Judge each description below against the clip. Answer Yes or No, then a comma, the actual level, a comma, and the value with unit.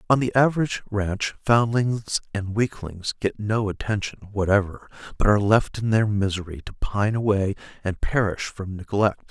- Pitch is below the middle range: Yes, low, 105 Hz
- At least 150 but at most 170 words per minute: Yes, average, 155 wpm